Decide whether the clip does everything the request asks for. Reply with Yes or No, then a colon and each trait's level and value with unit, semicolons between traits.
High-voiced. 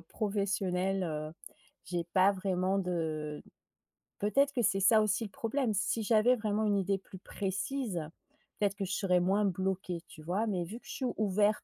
Yes: high, 195 Hz